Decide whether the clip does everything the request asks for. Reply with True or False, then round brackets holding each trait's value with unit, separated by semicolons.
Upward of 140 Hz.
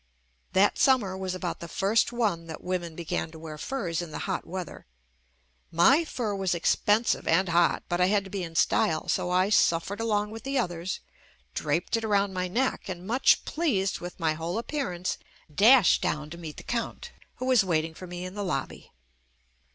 True (185 Hz)